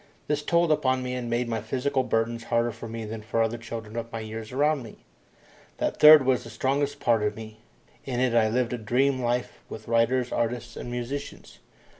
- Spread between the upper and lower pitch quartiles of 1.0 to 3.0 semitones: Yes, narrow, 2.4 semitones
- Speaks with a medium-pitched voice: No, low, 120 Hz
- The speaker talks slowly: No, fast, 205 wpm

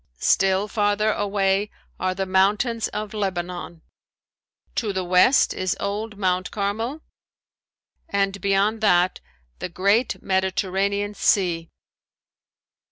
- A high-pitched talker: Yes, high, 200 Hz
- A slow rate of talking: Yes, slow, 100 wpm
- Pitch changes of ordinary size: No, narrow, 2.0 semitones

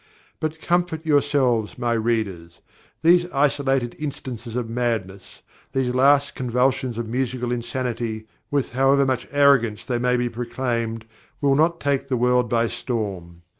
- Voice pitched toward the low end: Yes, low, 125 Hz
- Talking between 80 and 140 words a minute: Yes, slow, 135 wpm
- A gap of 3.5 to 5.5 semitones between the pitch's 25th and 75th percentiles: No, average, 3.1 semitones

